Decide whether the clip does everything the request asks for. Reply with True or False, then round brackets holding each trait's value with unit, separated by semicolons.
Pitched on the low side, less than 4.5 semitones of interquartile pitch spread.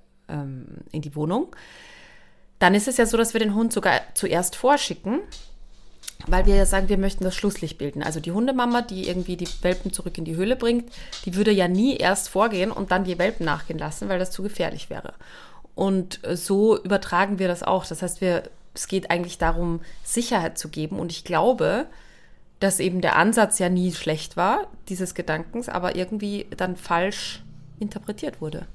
False (185 Hz; 3.3 semitones)